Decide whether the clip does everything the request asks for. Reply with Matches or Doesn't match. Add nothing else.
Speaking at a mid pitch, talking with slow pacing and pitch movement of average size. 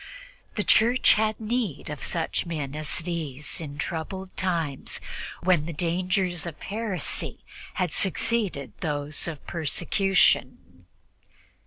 Matches